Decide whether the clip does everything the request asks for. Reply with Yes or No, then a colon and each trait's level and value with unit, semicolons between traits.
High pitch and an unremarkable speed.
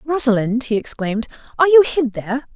Yes: very high, 255 Hz; average, 165 wpm